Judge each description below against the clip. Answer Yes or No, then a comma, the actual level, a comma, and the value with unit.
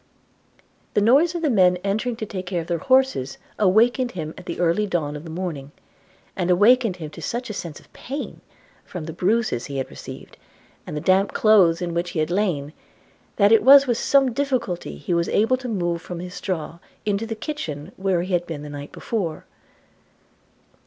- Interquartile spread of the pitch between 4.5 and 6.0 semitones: Yes, average, 5.2 semitones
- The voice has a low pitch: No, medium, 185 Hz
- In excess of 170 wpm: Yes, average, 195 wpm